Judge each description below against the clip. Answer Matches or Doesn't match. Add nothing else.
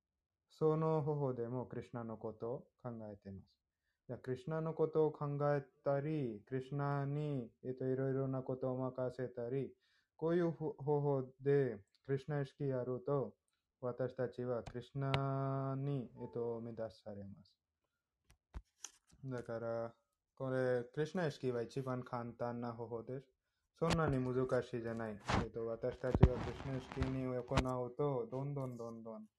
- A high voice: Doesn't match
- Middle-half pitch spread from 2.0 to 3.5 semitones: Matches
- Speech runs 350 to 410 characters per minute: Doesn't match